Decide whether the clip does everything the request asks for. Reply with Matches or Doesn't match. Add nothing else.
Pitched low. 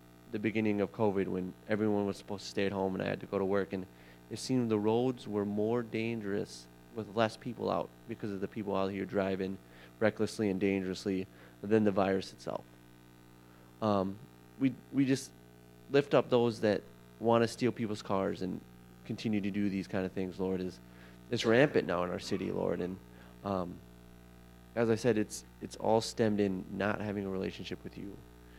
Matches